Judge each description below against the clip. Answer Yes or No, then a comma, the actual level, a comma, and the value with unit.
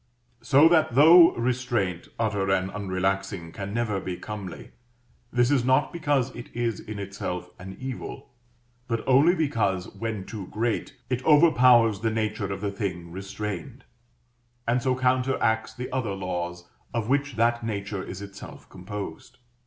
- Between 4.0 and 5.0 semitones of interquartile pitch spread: Yes, average, 4.7 semitones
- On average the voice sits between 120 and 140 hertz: No, low, 110 Hz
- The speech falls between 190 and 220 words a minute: No, average, 145 wpm